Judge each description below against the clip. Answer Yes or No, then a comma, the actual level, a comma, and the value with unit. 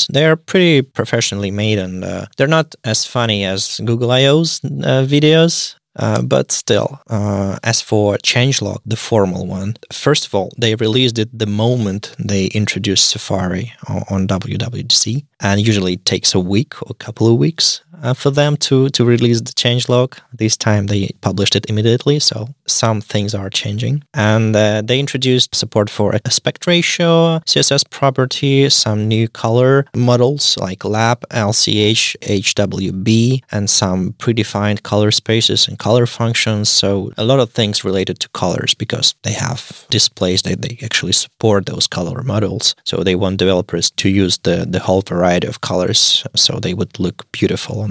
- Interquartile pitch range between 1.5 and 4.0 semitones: No, average, 4.5 semitones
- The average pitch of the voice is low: Yes, low, 110 Hz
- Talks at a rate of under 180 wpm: Yes, average, 170 wpm